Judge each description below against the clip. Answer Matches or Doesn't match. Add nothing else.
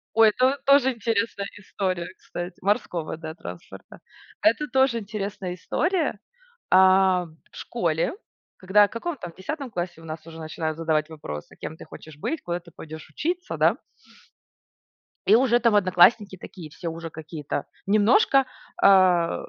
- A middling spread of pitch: Doesn't match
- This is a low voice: Doesn't match